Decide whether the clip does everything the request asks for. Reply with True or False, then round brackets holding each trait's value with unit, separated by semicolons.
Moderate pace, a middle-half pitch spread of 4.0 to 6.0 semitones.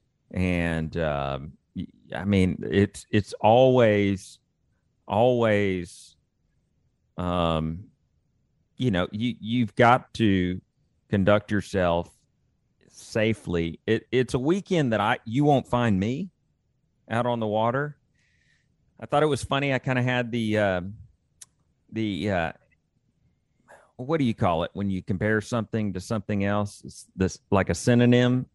False (130 wpm; 4.7 semitones)